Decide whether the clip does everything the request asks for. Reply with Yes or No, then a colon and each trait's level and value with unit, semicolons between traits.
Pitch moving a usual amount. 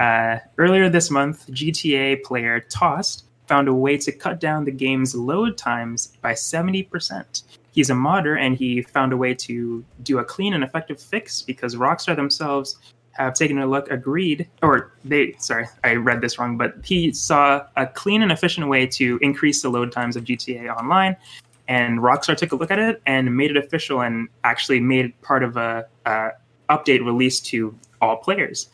Yes: average, 3.9 semitones